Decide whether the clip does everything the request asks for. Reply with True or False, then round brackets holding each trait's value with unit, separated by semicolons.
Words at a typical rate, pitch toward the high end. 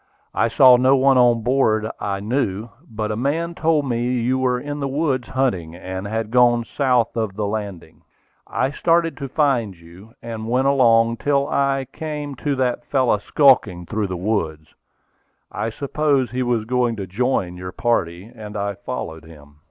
False (175 wpm; 120 Hz)